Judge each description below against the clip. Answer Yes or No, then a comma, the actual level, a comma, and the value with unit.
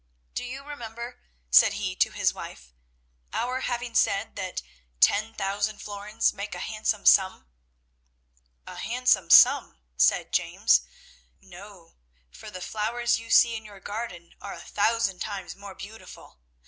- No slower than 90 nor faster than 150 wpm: Yes, average, 140 wpm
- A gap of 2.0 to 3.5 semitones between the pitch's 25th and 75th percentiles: Yes, average, 2.9 semitones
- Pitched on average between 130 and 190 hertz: No, high, 210 Hz